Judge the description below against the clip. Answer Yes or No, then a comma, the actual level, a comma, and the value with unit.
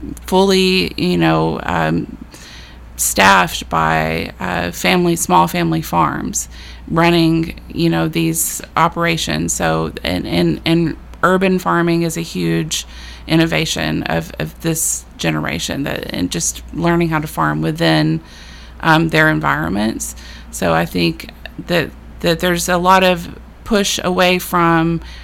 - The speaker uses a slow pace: Yes, slow, 125 wpm